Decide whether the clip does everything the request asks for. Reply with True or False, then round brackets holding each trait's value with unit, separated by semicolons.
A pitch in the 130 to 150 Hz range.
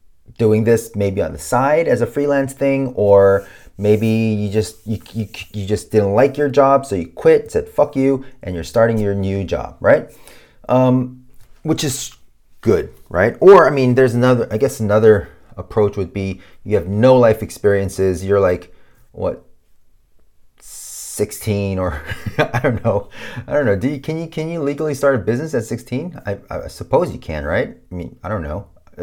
False (110 Hz)